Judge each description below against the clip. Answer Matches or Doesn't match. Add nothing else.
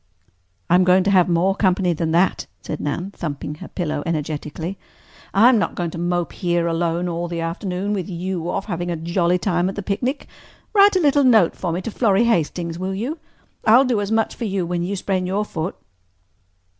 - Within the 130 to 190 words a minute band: Doesn't match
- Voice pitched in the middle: Matches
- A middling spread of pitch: Matches